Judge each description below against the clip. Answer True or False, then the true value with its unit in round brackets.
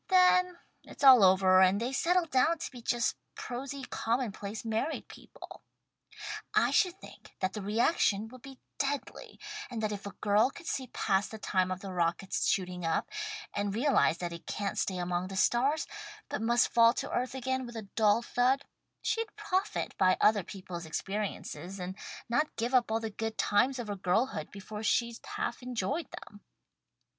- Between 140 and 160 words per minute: False (180 wpm)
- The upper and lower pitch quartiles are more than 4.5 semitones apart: True (5.0 semitones)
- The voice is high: True (225 Hz)